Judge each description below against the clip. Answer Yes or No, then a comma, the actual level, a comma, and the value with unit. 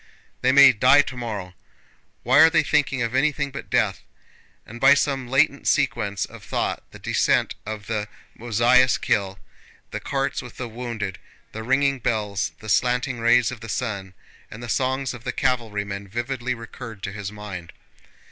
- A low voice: Yes, low, 120 Hz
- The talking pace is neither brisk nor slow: Yes, average, 165 wpm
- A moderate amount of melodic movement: Yes, average, 3.8 semitones